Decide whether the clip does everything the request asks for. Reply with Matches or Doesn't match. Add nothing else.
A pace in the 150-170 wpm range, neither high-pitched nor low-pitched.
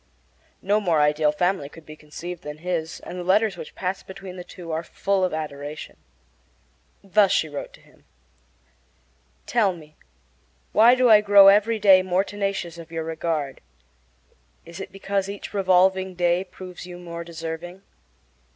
Matches